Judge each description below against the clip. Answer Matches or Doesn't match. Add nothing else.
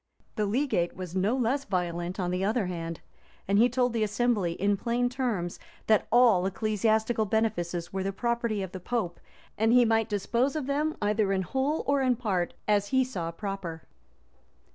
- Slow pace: Doesn't match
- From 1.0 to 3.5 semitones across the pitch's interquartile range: Doesn't match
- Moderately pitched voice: Doesn't match